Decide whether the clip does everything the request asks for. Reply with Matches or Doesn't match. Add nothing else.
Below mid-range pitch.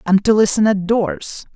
Doesn't match